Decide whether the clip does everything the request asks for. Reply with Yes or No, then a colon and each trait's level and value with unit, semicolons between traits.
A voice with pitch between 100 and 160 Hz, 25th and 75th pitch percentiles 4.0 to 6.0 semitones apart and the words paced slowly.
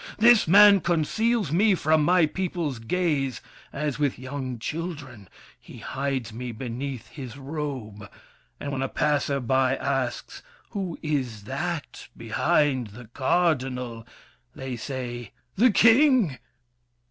Yes: medium, 140 Hz; average, 5.2 semitones; slow, 120 wpm